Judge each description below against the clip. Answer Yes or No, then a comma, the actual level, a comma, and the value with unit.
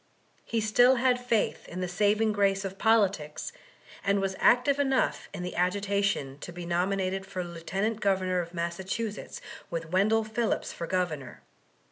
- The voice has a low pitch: No, high, 195 Hz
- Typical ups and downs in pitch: Yes, average, 3.5 semitones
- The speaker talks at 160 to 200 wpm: No, average, 150 wpm